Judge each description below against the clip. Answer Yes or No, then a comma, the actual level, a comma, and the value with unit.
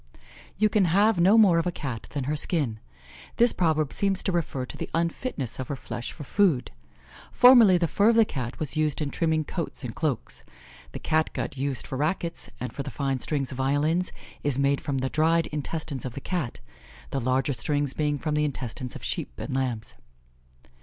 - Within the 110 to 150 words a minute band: No, average, 200 wpm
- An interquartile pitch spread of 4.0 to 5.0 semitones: Yes, average, 4.3 semitones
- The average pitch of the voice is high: No, medium, 150 Hz